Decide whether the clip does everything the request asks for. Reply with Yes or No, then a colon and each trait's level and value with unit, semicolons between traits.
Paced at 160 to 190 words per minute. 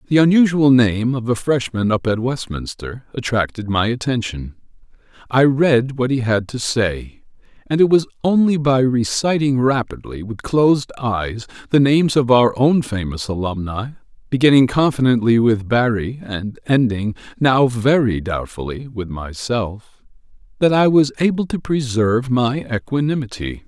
No: average, 140 wpm